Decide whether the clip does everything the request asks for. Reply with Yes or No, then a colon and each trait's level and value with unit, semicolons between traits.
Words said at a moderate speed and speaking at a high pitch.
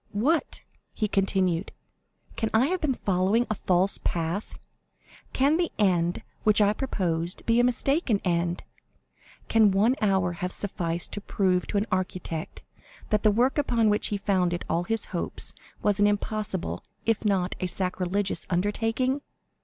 Yes: average, 145 wpm; high, 200 Hz